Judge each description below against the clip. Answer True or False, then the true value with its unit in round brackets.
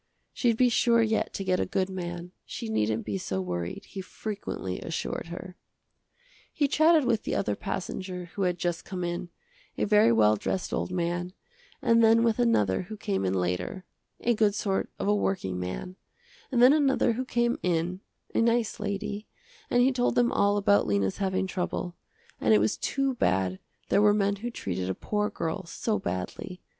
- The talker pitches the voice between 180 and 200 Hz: True (190 Hz)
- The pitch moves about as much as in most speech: False (5.7 semitones)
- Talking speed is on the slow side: False (185 wpm)